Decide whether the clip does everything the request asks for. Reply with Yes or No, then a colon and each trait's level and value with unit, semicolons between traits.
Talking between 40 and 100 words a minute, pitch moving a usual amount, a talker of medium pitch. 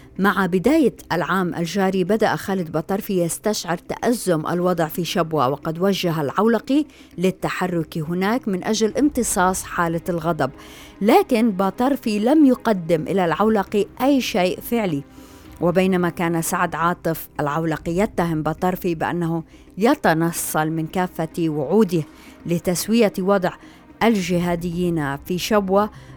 No: average, 110 wpm; average, 3.8 semitones; medium, 180 Hz